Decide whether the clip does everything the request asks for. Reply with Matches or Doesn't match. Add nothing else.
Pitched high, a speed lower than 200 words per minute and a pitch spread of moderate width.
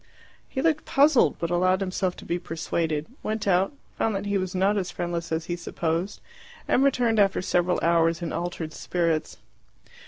Doesn't match